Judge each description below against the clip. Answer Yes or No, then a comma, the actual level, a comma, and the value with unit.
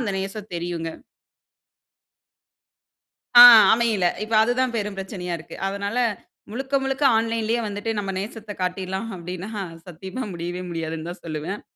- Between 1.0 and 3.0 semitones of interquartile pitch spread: No, average, 4.1 semitones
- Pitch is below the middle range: No, high, 195 Hz